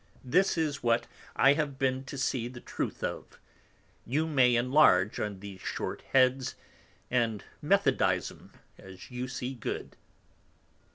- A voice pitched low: Yes, low, 125 Hz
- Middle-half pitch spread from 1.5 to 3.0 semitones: Yes, narrow, 2.6 semitones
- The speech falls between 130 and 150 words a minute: Yes, slow, 135 wpm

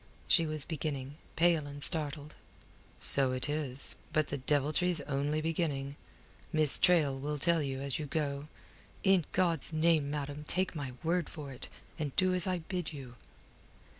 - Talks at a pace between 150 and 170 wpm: Yes, average, 160 wpm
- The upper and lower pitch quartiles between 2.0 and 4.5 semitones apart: Yes, average, 2.8 semitones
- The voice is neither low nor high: Yes, medium, 150 Hz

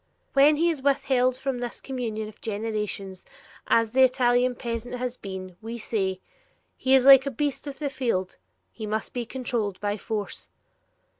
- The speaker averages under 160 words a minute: No, average, 165 wpm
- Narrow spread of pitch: No, average, 3.7 semitones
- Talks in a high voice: Yes, high, 240 Hz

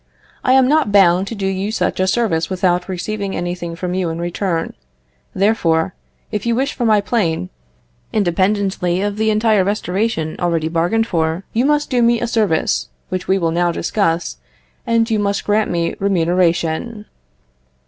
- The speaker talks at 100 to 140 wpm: No, average, 160 wpm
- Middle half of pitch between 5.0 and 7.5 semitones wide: No, average, 4.0 semitones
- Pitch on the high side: Yes, high, 195 Hz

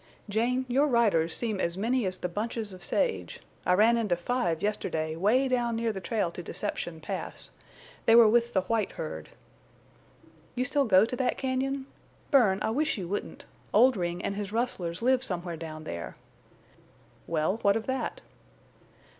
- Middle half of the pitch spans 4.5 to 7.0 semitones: Yes, wide, 5.6 semitones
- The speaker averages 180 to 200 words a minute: No, average, 165 wpm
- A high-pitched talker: Yes, high, 215 Hz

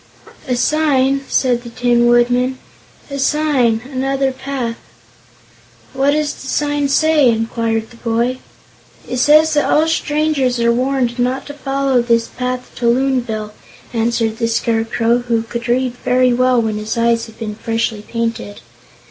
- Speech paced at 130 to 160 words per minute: Yes, average, 150 wpm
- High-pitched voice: Yes, high, 245 Hz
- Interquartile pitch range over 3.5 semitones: No, average, 2.7 semitones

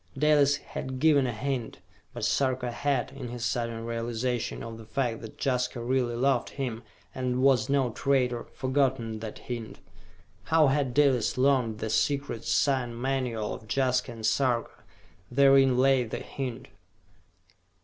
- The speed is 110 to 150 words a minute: Yes, average, 145 wpm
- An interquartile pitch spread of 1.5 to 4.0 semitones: Yes, narrow, 2.6 semitones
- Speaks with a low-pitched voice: Yes, low, 125 Hz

